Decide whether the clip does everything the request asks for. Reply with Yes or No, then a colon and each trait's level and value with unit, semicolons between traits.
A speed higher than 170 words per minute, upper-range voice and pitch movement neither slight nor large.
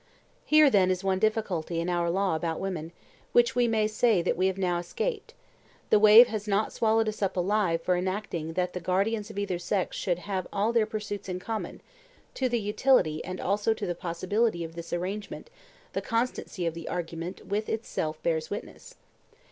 Yes: average, 190 wpm; high, 195 Hz; average, 3.7 semitones